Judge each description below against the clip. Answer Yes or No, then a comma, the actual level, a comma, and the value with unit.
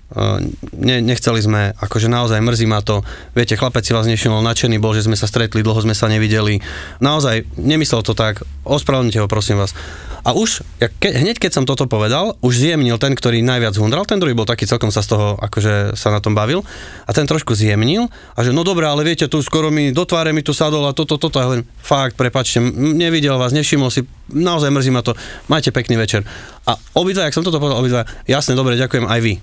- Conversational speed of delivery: No, fast, 225 wpm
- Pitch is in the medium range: No, low, 120 Hz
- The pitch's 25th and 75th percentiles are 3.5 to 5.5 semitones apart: Yes, average, 4.8 semitones